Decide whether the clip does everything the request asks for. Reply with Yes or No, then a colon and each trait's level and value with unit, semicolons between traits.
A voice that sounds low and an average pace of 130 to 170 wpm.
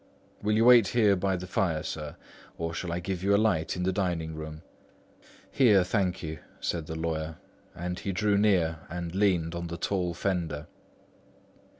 No: very low, 90 Hz; average, 180 wpm